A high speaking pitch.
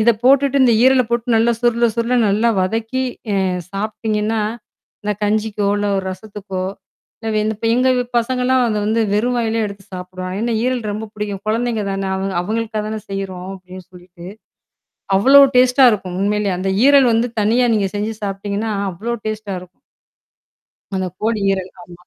Yes: high, 215 Hz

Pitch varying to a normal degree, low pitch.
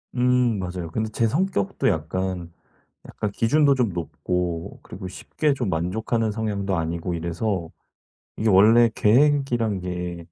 Yes: average, 4.9 semitones; low, 100 Hz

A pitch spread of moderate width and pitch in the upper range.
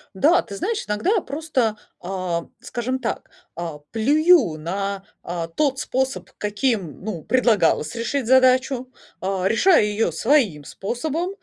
No: wide, 6.2 semitones; high, 225 Hz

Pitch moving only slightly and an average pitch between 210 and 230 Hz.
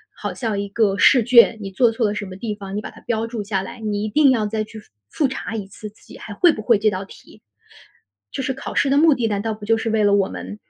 Yes: narrow, 2.3 semitones; high, 215 Hz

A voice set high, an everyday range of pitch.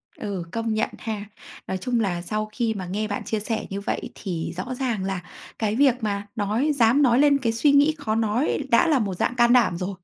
Yes: high, 220 Hz; average, 3.7 semitones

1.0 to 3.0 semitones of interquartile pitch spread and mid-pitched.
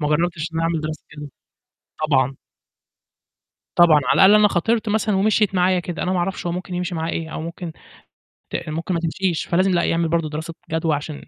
Yes: narrow, 2.6 semitones; medium, 170 Hz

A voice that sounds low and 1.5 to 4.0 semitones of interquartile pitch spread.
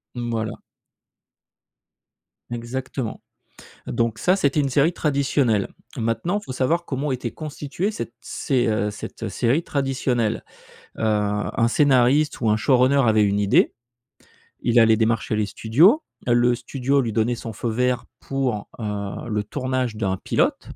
Yes: low, 120 Hz; average, 3.7 semitones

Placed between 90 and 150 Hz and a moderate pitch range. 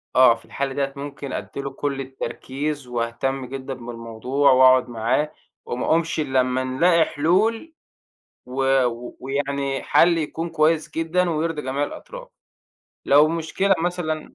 Yes: medium, 140 Hz; average, 3.7 semitones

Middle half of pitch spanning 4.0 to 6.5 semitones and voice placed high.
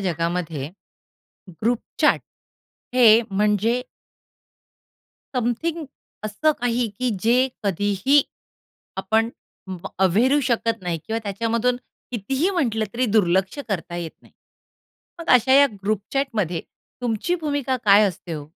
Yes: average, 4.7 semitones; high, 220 Hz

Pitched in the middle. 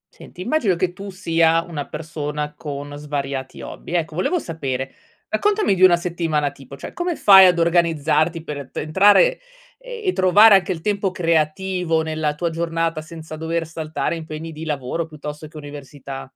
Yes: medium, 165 Hz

